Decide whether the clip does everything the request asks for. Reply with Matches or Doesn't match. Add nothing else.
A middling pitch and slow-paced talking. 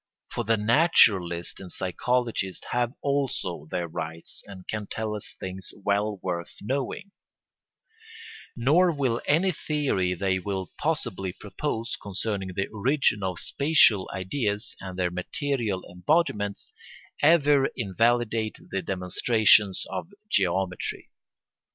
Doesn't match